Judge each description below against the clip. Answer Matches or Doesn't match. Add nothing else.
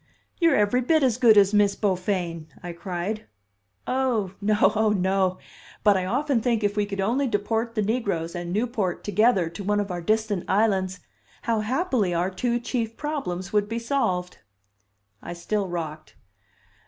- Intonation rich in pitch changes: Doesn't match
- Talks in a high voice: Matches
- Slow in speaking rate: Doesn't match